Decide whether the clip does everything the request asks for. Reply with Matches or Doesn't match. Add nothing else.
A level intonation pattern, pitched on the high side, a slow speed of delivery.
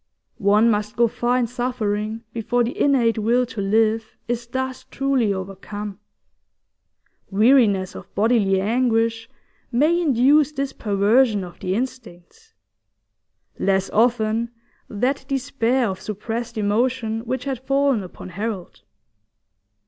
Doesn't match